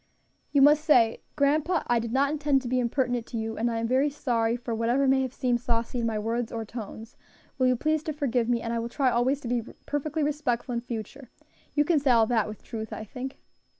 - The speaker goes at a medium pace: No, fast, 240 wpm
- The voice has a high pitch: Yes, high, 245 Hz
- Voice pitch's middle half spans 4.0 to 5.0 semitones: No, average, 3.4 semitones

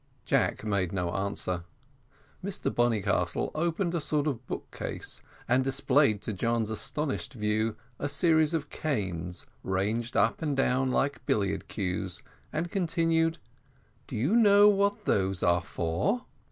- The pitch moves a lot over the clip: Yes, wide, 8.3 semitones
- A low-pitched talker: Yes, low, 125 Hz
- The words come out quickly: No, average, 140 wpm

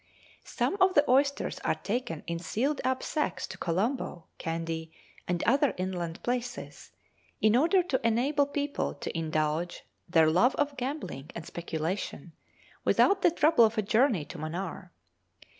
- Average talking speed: Yes, average, 145 wpm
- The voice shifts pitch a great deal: Yes, wide, 8.8 semitones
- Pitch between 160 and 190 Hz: No, high, 220 Hz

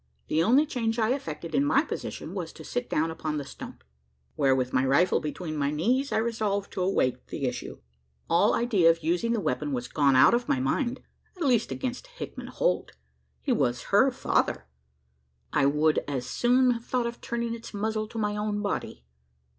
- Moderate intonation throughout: No, wide, 8.0 semitones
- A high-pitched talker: Yes, high, 205 Hz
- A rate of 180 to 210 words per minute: Yes, average, 195 wpm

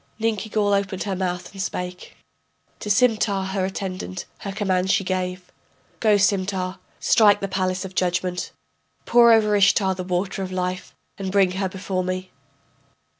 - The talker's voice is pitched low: No, high, 190 Hz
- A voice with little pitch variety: Yes, narrow, 1.6 semitones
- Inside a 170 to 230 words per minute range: No, average, 150 wpm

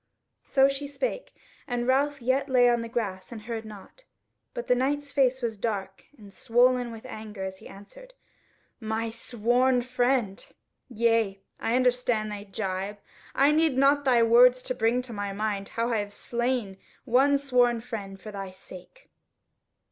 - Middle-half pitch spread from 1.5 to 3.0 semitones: No, average, 3.5 semitones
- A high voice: Yes, high, 240 Hz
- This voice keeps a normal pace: Yes, average, 165 wpm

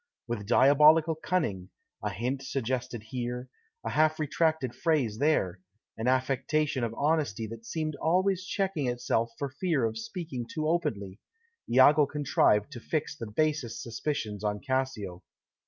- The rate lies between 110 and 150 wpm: Yes, average, 140 wpm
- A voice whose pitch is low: Yes, low, 130 Hz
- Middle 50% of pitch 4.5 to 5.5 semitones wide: Yes, average, 5.2 semitones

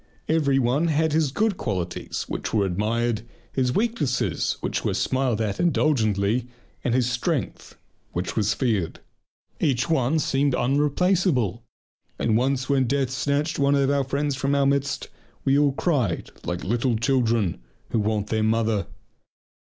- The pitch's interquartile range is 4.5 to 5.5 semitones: No, average, 4.1 semitones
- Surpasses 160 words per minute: No, average, 145 wpm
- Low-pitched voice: Yes, low, 130 Hz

